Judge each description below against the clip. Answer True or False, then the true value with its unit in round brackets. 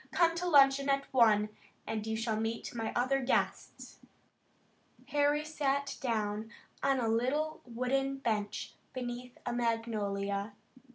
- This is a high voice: True (245 Hz)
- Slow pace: True (125 wpm)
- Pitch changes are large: False (3.7 semitones)